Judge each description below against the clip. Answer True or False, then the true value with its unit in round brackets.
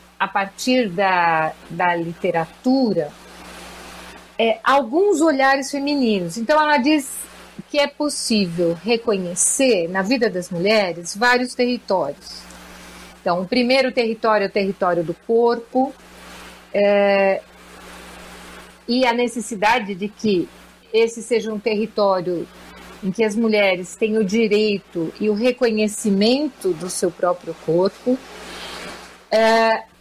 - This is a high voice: True (215 Hz)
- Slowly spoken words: True (110 wpm)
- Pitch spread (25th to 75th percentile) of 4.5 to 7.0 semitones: True (5.2 semitones)